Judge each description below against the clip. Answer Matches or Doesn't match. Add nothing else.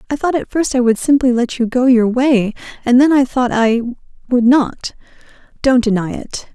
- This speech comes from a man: Doesn't match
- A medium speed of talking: Matches